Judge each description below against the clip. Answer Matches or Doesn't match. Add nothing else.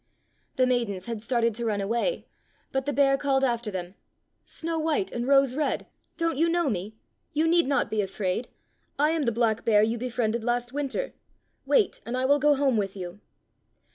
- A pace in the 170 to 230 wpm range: Matches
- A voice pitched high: Matches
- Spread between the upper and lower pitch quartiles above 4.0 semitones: Matches